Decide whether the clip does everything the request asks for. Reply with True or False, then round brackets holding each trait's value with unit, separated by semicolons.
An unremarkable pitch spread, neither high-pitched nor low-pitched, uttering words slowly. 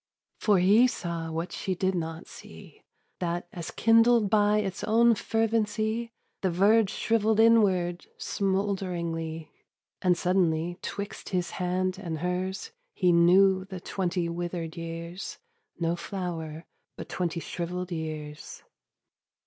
True (3.2 semitones; 180 Hz; 120 wpm)